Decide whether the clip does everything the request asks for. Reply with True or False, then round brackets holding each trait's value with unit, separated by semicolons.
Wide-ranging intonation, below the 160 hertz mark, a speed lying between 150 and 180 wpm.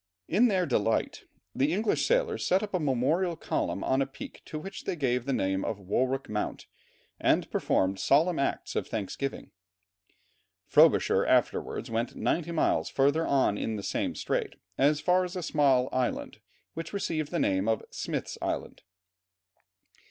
True (6.2 semitones; 140 Hz; 160 wpm)